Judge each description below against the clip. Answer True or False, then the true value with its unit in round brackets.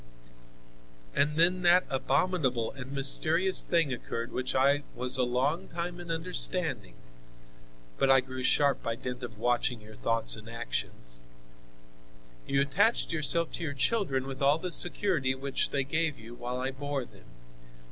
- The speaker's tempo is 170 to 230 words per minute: False (155 wpm)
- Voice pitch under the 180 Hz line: True (135 Hz)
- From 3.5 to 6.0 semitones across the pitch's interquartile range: True (4.8 semitones)